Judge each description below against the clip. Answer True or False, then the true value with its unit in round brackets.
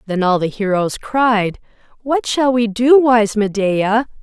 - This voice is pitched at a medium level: False (225 Hz)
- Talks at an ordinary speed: True (155 wpm)